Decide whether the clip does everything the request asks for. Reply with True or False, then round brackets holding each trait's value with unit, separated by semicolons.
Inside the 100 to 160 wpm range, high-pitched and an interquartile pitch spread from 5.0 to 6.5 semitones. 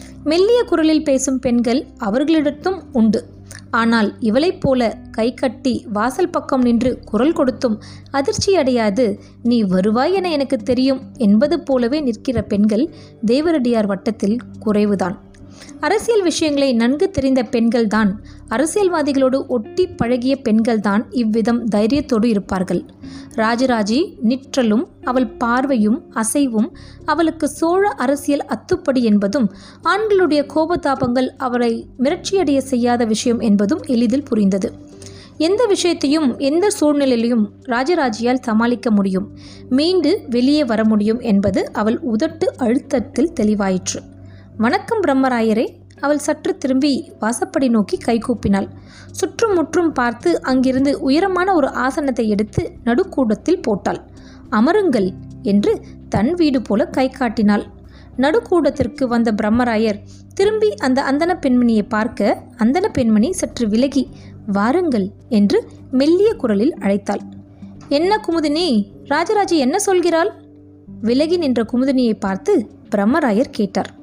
True (105 wpm; 255 Hz; 5.5 semitones)